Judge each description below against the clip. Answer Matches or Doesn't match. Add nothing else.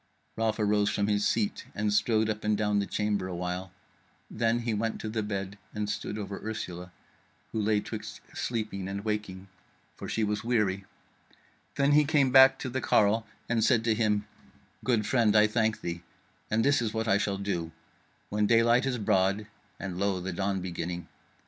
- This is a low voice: Matches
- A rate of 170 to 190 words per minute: Matches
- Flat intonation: Matches